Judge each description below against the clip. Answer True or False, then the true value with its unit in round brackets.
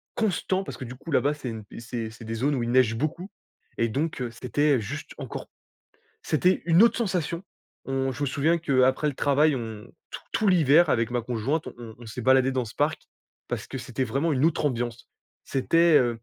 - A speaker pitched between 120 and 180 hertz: True (135 Hz)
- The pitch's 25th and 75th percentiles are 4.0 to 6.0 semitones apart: True (4.7 semitones)